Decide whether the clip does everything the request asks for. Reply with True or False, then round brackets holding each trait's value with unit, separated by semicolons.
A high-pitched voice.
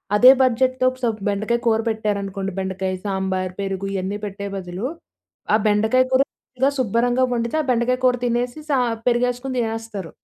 True (225 Hz)